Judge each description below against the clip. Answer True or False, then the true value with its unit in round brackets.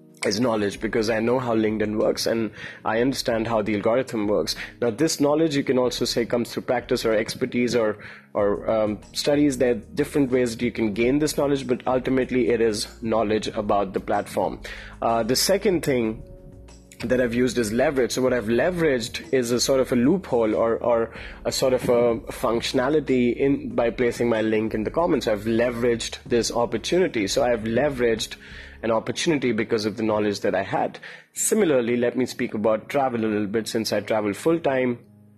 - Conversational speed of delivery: True (190 wpm)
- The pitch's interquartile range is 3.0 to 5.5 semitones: False (2.6 semitones)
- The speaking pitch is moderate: False (120 Hz)